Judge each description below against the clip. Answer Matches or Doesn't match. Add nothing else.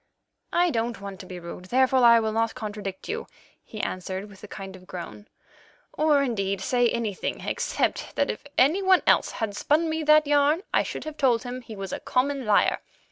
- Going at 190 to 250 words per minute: Matches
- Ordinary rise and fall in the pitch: Doesn't match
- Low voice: Doesn't match